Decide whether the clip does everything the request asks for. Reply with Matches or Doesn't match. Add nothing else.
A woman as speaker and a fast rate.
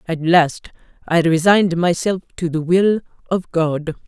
Doesn't match